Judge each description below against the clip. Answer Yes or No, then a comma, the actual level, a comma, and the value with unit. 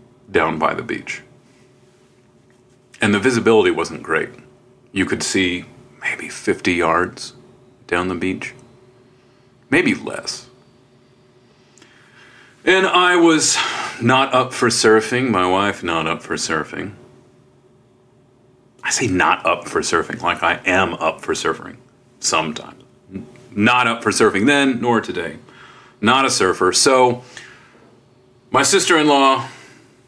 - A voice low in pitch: Yes, low, 125 Hz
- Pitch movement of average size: No, narrow, 1.7 semitones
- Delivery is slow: Yes, slow, 120 wpm